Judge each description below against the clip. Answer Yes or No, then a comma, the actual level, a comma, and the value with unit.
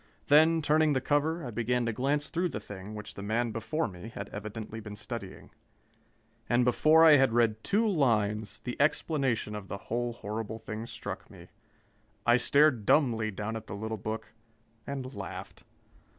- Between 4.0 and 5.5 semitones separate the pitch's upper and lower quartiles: Yes, average, 5.0 semitones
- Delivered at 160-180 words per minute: Yes, average, 170 wpm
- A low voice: Yes, low, 115 Hz